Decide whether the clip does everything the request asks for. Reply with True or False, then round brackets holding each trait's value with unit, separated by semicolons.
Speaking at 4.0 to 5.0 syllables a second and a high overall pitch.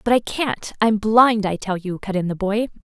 True (4.8 syllables/s; 210 Hz)